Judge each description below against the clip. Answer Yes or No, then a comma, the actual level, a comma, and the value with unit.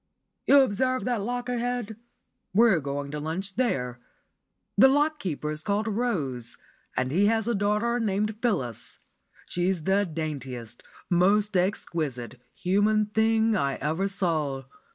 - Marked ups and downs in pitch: Yes, wide, 6.6 semitones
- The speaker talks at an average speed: No, slow, 130 wpm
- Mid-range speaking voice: No, high, 195 Hz